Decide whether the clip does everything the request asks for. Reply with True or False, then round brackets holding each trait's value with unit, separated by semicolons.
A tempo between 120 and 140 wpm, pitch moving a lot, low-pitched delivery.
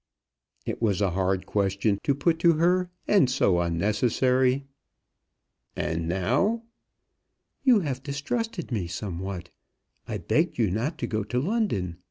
True (135 wpm; 8.8 semitones; 120 Hz)